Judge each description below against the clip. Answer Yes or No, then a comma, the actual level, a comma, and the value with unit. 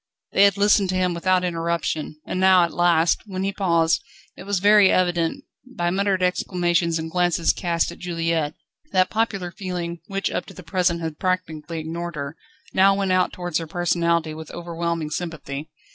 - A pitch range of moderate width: No, narrow, 2.0 semitones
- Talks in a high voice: No, medium, 175 Hz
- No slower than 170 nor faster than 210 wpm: Yes, average, 175 wpm